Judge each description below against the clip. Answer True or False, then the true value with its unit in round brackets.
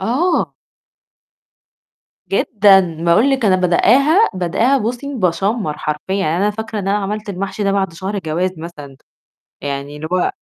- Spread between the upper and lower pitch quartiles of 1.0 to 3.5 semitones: False (4.5 semitones)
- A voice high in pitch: True (195 Hz)